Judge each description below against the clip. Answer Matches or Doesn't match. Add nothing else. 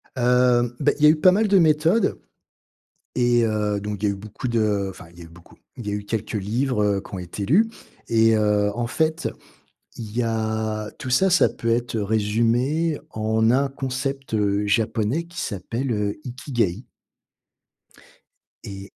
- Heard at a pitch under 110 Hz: Doesn't match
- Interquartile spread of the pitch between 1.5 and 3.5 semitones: Doesn't match